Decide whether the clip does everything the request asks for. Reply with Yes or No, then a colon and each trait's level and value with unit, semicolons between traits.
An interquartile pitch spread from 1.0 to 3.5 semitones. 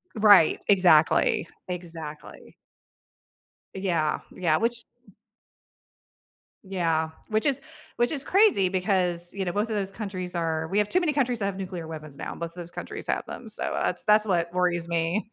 No: average, 3.9 semitones